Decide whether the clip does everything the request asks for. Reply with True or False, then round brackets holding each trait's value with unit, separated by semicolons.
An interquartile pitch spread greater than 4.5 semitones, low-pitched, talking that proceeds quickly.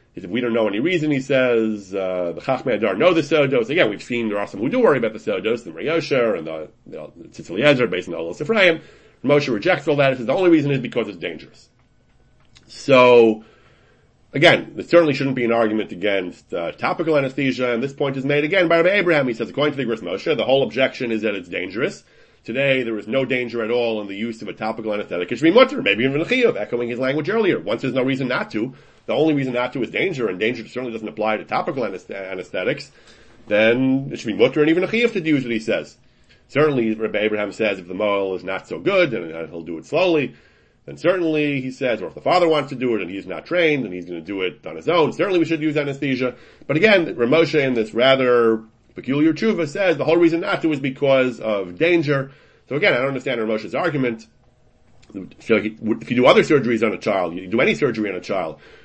True (5.2 semitones; 130 Hz; 240 wpm)